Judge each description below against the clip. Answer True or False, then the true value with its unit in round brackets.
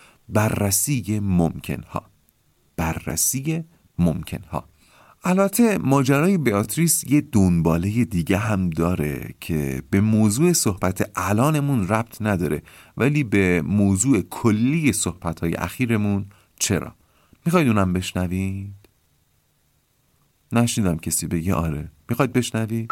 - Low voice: True (100 Hz)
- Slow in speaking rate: True (95 wpm)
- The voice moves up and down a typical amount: False (6.2 semitones)